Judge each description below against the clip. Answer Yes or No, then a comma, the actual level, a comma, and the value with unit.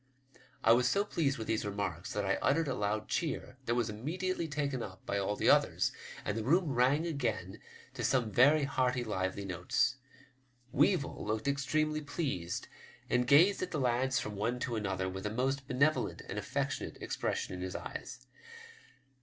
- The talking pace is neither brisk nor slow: Yes, average, 175 wpm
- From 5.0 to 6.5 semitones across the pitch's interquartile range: Yes, wide, 5.4 semitones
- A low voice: Yes, low, 125 Hz